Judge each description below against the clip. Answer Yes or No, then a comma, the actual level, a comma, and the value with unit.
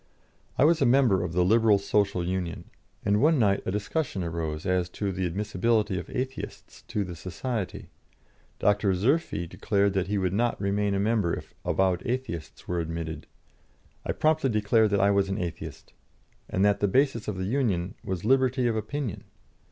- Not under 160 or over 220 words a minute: Yes, average, 175 wpm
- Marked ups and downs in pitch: No, average, 4.1 semitones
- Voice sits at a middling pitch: No, low, 100 Hz